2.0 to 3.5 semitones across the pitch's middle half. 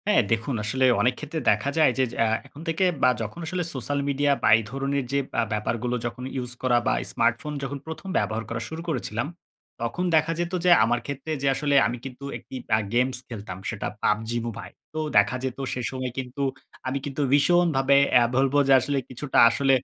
Yes: average, 3.2 semitones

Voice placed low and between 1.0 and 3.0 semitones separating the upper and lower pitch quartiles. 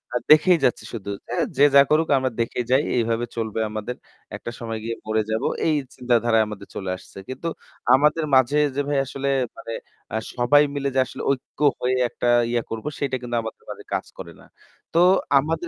No: low, 125 Hz; average, 3.9 semitones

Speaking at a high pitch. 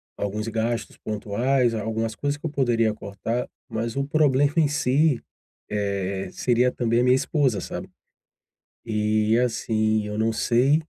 No: low, 115 Hz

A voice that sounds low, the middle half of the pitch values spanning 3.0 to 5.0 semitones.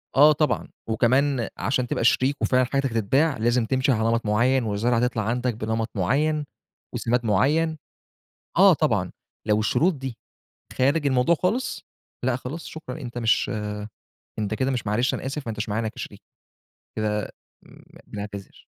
Yes: low, 125 Hz; average, 3.7 semitones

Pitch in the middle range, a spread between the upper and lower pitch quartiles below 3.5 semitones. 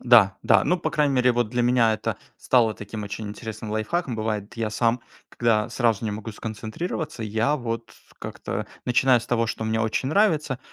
No: low, 115 Hz; narrow, 2.6 semitones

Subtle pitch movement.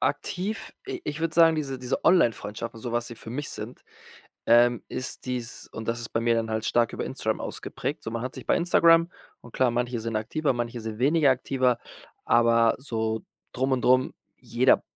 No: average, 3.1 semitones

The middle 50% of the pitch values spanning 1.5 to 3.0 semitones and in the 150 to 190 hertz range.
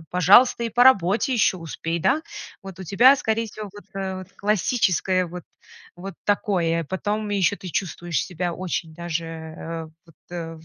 No: average, 3.6 semitones; medium, 185 Hz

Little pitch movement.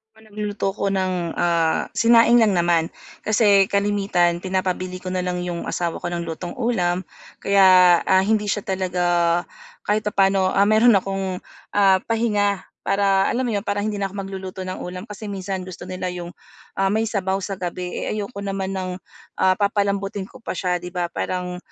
Yes: narrow, 2.0 semitones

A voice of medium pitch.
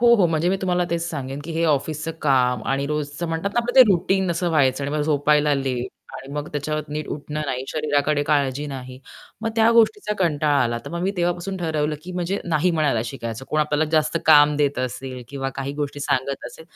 Yes: medium, 150 Hz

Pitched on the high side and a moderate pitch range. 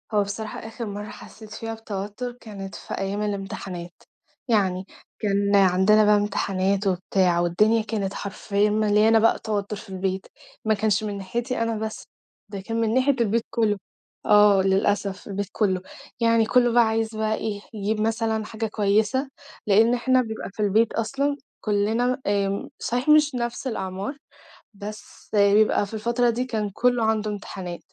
No: high, 210 Hz; narrow, 2.2 semitones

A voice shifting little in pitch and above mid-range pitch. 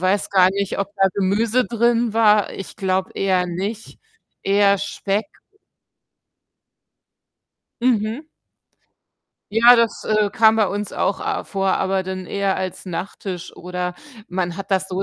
Yes: narrow, 2.3 semitones; high, 195 Hz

